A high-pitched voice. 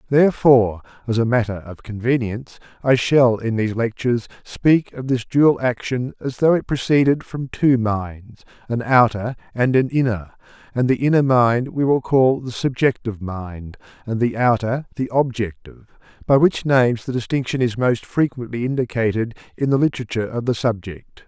No: low, 120 Hz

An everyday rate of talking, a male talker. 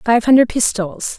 No: average, 150 wpm; female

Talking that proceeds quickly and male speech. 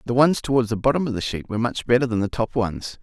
Yes: fast, 300 wpm; male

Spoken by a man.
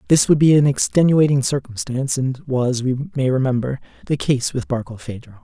Yes: male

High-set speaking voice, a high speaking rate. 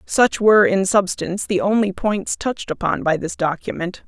No: high, 195 Hz; average, 175 wpm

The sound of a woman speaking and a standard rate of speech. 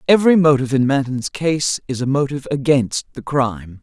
Yes: female; average, 175 wpm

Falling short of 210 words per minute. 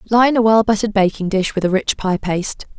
No: fast, 235 wpm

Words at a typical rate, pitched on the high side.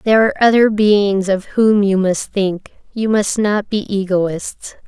Yes: average, 170 wpm; high, 200 Hz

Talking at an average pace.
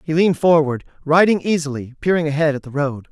Yes: average, 195 wpm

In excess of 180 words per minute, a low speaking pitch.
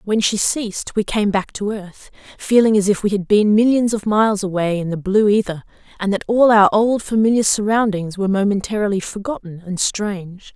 No: average, 195 wpm; high, 205 Hz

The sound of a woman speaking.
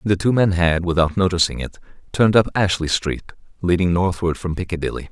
No: male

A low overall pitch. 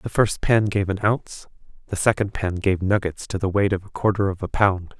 Yes: low, 100 Hz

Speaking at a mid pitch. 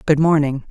Yes: medium, 150 Hz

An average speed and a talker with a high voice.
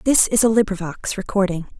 Yes: average, 165 wpm; high, 200 Hz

